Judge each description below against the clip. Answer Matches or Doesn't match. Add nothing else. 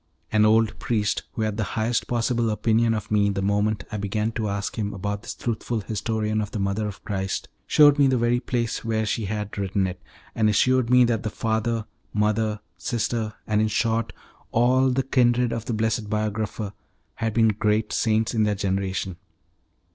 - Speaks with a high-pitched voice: Doesn't match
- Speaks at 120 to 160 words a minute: Doesn't match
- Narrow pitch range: Matches